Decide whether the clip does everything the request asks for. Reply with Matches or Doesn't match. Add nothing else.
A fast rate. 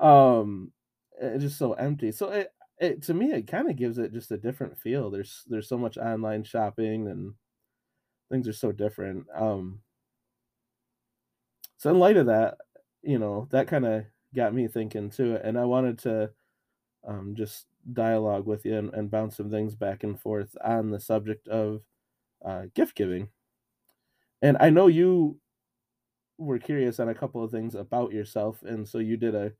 Doesn't match